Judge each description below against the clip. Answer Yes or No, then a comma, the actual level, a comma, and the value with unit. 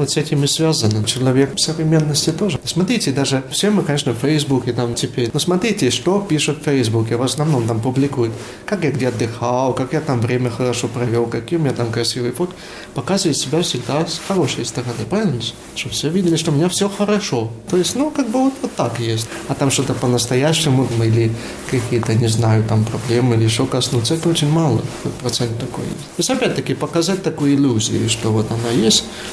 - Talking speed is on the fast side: Yes, fast, 195 wpm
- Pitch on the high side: No, low, 135 Hz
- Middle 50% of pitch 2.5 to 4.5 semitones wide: No, average, 5.2 semitones